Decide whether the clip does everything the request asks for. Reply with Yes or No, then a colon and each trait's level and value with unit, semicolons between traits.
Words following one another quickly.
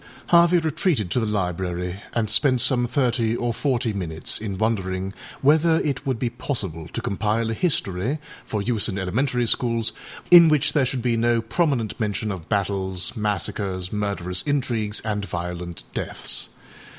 No: average, 160 wpm